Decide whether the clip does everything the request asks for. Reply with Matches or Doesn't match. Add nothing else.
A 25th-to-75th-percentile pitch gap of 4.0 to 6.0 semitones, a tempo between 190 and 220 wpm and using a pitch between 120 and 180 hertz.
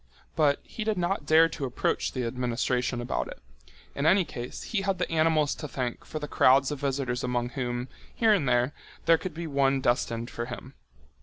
Matches